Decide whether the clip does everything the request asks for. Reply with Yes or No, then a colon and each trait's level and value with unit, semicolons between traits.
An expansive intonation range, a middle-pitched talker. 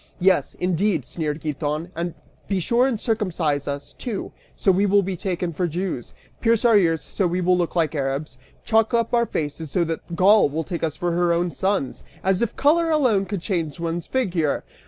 No: average, 4.0 semitones; medium, 180 Hz